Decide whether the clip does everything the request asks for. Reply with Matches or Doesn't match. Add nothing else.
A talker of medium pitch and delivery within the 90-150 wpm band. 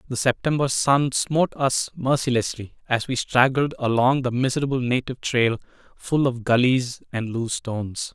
Doesn't match